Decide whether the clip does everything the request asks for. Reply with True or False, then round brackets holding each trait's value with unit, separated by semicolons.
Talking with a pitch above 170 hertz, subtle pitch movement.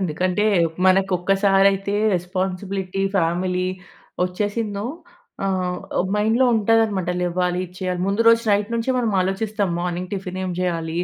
True (190 Hz; 2.1 semitones)